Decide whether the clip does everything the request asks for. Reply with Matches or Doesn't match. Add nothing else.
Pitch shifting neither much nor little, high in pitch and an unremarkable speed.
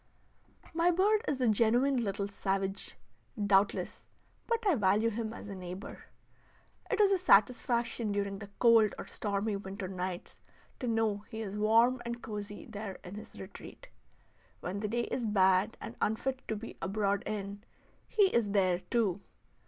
Matches